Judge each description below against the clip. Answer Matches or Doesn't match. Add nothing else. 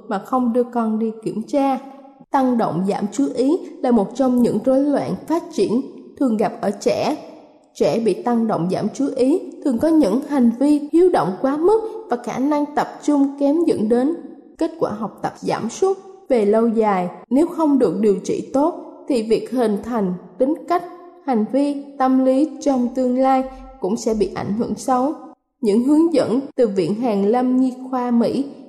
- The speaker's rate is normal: Matches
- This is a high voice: Matches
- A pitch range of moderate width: Matches